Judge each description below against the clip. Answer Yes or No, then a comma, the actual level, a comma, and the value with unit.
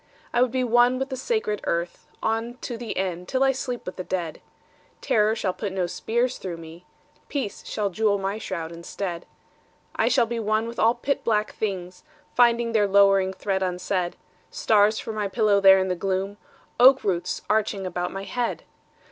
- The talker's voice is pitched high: Yes, high, 205 Hz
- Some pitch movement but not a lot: Yes, average, 3.9 semitones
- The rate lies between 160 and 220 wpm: Yes, average, 185 wpm